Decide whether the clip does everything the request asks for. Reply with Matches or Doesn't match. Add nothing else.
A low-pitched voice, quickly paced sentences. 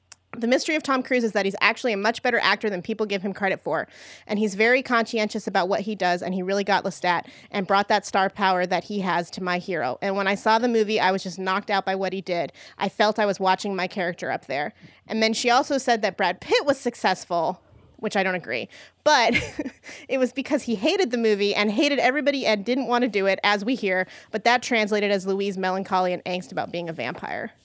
Doesn't match